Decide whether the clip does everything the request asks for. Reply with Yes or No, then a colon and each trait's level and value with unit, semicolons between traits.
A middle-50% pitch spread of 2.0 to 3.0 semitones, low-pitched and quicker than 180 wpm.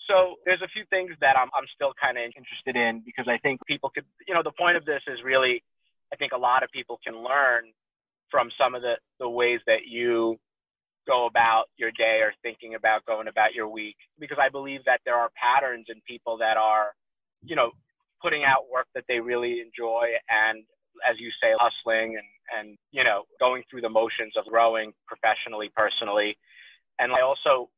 Yes: narrow, 2.6 semitones; low, 115 Hz; average, 200 wpm